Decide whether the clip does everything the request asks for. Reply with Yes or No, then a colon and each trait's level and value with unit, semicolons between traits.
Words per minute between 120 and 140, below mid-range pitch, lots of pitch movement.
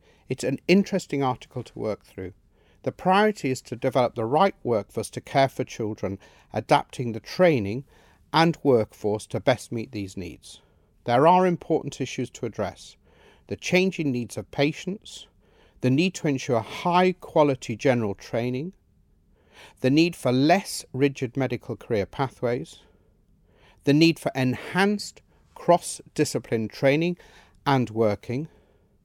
Yes: slow, 135 wpm; low, 130 Hz; wide, 6.3 semitones